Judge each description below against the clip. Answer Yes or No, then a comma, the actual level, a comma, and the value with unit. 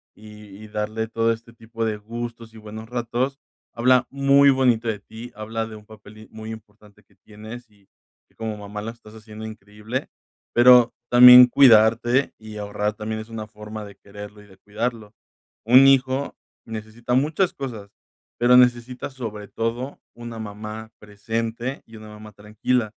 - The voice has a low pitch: Yes, low, 110 Hz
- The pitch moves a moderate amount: No, narrow, 2.3 semitones